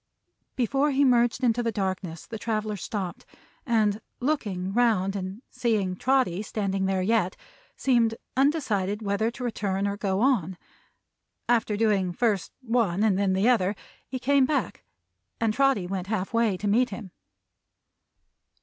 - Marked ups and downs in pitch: No, average, 3.9 semitones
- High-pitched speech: Yes, high, 215 Hz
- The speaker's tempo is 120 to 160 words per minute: Yes, average, 150 wpm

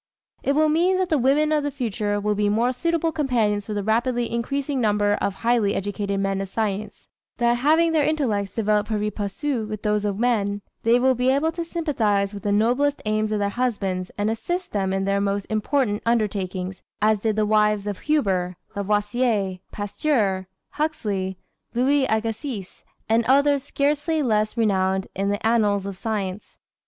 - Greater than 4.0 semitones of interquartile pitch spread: Yes, average, 4.6 semitones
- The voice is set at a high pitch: Yes, high, 215 Hz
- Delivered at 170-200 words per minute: Yes, average, 175 wpm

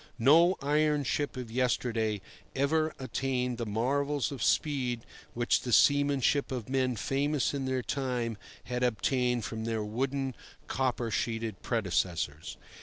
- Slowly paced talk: Yes, slow, 130 wpm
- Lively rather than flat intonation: No, average, 3.3 semitones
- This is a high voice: No, low, 125 Hz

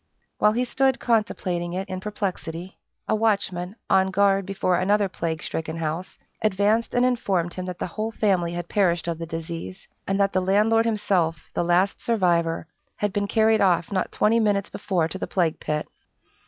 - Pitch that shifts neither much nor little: Yes, average, 3.4 semitones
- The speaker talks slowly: No, average, 180 wpm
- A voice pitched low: No, high, 190 Hz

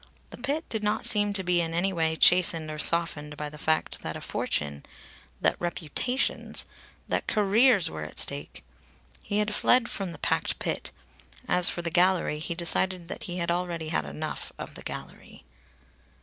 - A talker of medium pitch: Yes, medium, 175 Hz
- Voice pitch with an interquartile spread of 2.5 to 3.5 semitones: No, average, 4.1 semitones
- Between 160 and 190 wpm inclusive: Yes, average, 180 wpm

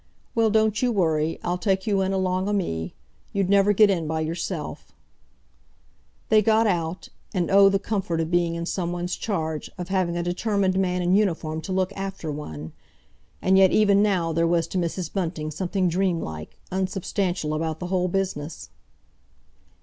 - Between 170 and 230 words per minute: Yes, average, 175 wpm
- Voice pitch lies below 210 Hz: Yes, medium, 185 Hz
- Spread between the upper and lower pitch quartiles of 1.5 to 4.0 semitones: Yes, average, 2.9 semitones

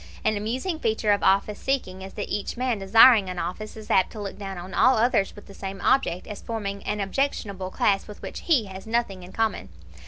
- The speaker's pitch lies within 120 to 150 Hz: No, high, 205 Hz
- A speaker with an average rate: No, fast, 220 wpm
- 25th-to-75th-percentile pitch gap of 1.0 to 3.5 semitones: Yes, average, 2.8 semitones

